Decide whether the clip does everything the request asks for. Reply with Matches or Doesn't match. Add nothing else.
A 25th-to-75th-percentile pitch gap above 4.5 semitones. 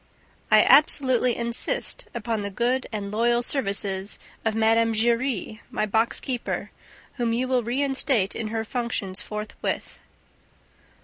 Doesn't match